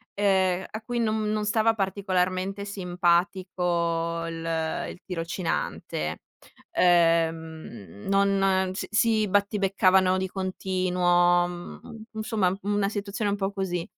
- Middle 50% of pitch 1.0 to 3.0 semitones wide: Yes, narrow, 2.5 semitones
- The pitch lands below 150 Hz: No, medium, 185 Hz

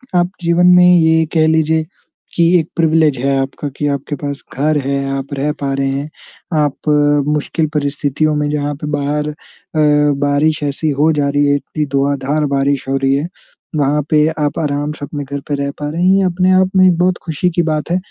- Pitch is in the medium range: Yes, medium, 150 Hz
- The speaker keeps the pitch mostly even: Yes, narrow, 2.1 semitones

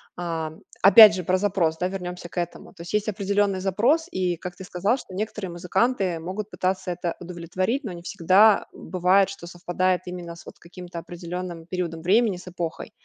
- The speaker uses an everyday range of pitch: No, narrow, 2.2 semitones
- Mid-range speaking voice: Yes, medium, 180 Hz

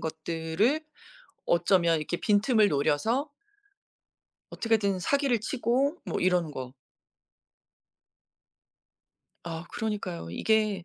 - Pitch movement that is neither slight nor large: No, wide, 5.8 semitones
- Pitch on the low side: No, high, 195 Hz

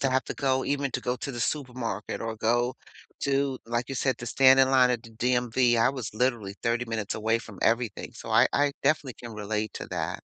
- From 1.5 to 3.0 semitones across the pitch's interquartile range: Yes, narrow, 2.6 semitones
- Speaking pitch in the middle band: No, low, 120 Hz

